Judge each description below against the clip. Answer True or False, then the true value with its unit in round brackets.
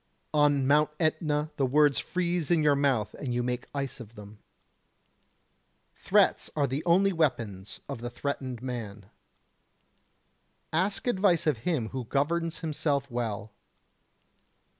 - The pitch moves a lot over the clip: False (4.6 semitones)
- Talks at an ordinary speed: False (130 wpm)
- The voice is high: False (140 Hz)